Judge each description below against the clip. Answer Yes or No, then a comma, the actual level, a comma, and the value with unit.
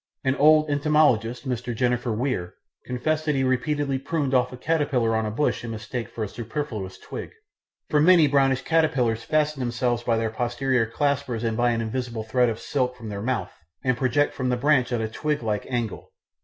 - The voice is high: No, low, 125 Hz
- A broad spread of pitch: No, average, 3.8 semitones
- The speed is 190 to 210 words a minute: Yes, average, 195 wpm